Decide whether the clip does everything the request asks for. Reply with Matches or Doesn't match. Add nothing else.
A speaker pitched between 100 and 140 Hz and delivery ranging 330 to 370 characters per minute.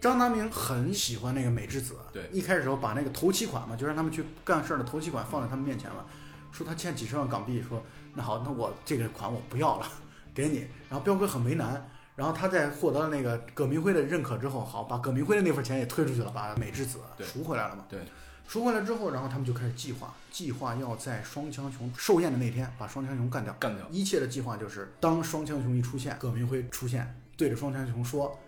Matches